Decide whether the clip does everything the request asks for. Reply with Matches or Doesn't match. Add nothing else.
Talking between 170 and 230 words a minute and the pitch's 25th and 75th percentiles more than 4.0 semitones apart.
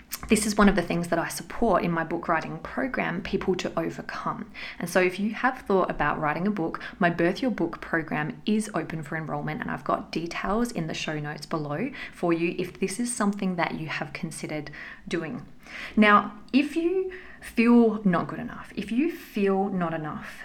Matches